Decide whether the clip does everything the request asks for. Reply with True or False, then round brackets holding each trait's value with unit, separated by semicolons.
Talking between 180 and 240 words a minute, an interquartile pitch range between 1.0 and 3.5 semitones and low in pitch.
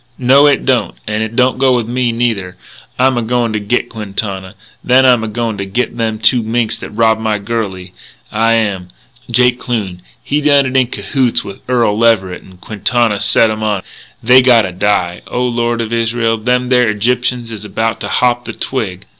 True (195 wpm; 2.9 semitones; 115 Hz)